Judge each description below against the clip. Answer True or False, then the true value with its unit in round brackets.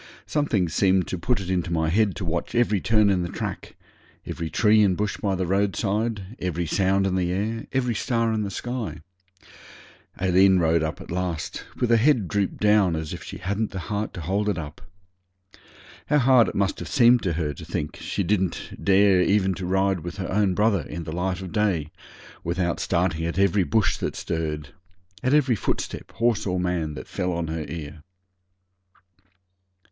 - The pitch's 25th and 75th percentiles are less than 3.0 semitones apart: False (3.6 semitones)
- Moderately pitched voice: False (95 Hz)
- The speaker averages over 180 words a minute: True (190 wpm)